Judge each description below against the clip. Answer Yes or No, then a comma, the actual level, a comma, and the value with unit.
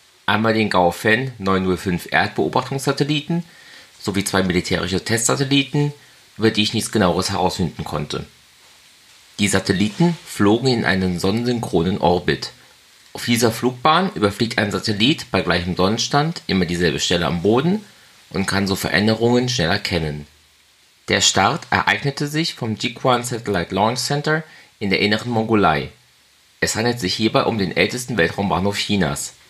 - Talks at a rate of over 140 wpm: No, average, 135 wpm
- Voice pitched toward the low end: Yes, low, 105 Hz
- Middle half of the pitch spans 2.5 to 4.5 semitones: No, average, 5.3 semitones